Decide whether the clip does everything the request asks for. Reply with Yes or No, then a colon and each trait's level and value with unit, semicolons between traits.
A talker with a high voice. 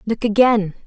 Yes: high, 215 Hz